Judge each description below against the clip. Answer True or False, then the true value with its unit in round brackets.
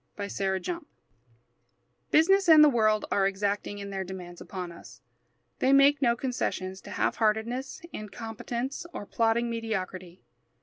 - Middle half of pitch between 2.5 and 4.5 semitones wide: False (4.9 semitones)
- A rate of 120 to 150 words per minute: True (140 wpm)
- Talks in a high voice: True (220 Hz)